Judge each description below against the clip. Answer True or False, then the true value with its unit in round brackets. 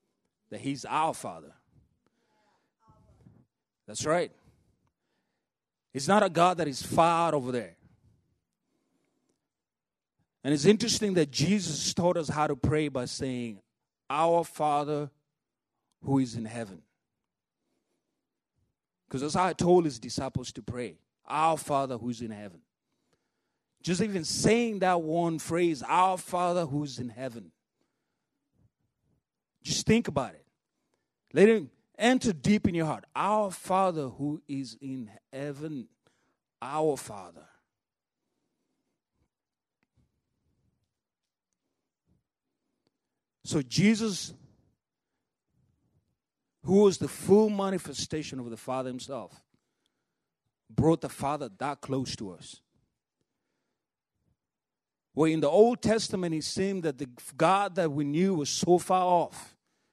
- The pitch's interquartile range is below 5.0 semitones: False (5.3 semitones)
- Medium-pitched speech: True (155 Hz)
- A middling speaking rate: False (115 wpm)